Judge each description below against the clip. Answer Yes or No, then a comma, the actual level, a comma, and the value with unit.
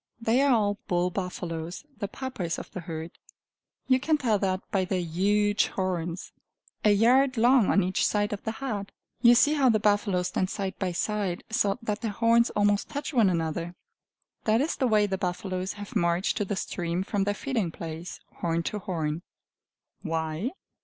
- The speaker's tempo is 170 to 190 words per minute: Yes, average, 180 wpm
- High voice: Yes, high, 200 Hz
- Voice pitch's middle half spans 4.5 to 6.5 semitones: No, average, 3.9 semitones